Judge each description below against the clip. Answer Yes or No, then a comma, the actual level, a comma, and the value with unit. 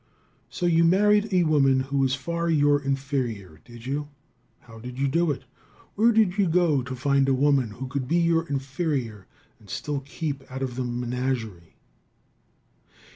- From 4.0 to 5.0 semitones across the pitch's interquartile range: Yes, average, 4.4 semitones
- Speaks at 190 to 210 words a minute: No, average, 170 wpm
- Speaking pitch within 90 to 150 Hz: Yes, medium, 140 Hz